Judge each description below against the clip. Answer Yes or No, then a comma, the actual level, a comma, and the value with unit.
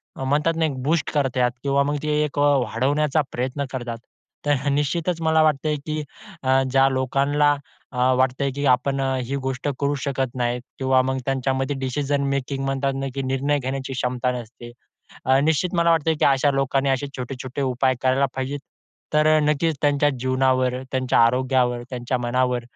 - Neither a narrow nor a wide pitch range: No, narrow, 1.9 semitones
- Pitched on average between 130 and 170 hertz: Yes, low, 135 Hz